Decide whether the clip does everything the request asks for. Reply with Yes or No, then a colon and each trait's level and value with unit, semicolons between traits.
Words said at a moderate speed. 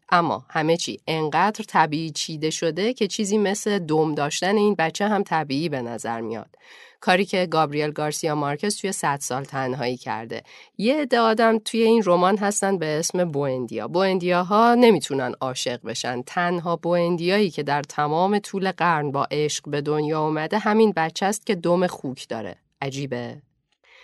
No: fast, 160 wpm